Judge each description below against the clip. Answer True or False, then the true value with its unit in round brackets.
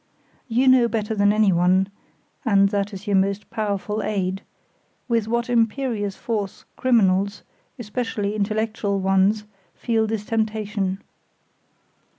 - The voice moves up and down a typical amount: False (2.2 semitones)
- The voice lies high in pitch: True (210 Hz)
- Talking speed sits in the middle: False (115 wpm)